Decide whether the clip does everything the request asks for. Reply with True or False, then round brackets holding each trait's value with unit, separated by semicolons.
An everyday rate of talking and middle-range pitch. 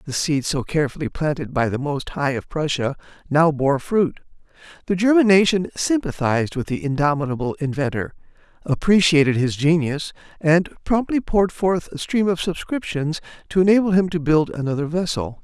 True (155 wpm; 160 Hz)